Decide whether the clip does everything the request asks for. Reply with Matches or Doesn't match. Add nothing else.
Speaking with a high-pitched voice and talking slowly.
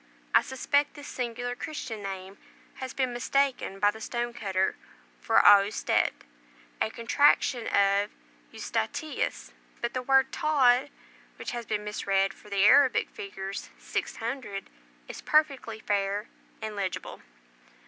Matches